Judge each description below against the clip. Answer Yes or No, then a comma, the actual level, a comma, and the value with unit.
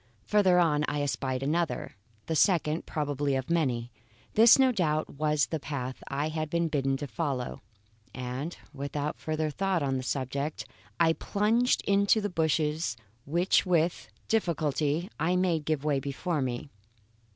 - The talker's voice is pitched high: No, medium, 155 Hz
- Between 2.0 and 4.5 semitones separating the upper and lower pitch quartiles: Yes, average, 3.5 semitones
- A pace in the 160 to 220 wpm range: No, average, 150 wpm